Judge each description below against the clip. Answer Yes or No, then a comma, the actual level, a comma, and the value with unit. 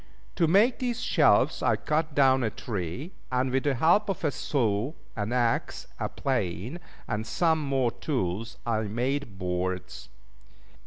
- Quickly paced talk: No, average, 150 wpm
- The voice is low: Yes, low, 130 Hz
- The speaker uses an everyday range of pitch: No, wide, 6.2 semitones